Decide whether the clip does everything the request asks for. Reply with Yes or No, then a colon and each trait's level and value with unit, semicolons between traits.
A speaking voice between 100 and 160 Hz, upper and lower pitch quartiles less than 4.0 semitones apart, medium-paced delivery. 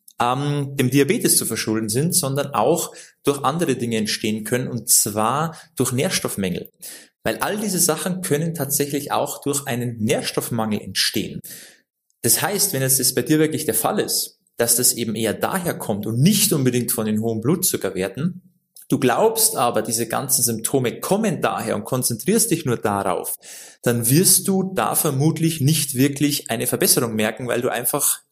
No: low, 135 Hz; average, 4.9 semitones; average, 160 wpm